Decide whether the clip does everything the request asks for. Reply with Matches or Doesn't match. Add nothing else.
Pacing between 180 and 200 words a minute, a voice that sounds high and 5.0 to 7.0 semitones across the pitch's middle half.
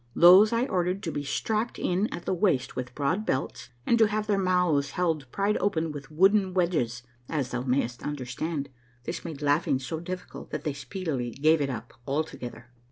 Doesn't match